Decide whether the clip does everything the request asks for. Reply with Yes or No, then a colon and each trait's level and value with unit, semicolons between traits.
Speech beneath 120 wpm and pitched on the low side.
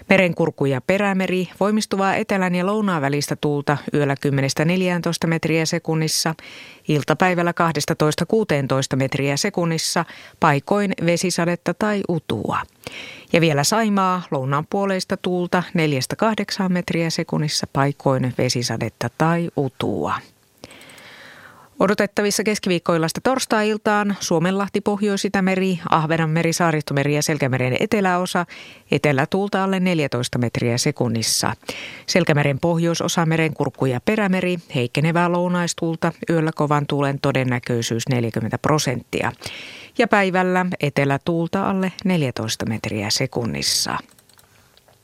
No: slow, 95 wpm; medium, 165 Hz